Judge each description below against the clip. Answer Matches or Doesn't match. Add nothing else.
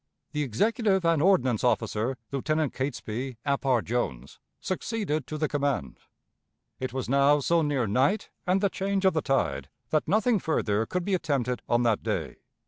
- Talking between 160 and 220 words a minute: Matches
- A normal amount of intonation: Doesn't match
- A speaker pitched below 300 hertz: Matches